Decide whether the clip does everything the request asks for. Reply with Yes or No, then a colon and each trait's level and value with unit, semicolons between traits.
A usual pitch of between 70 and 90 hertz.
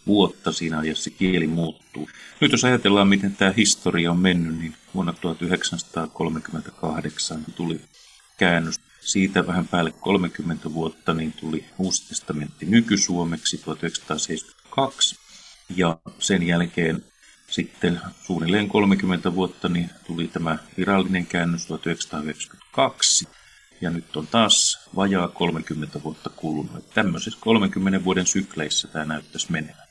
Yes: very low, 85 Hz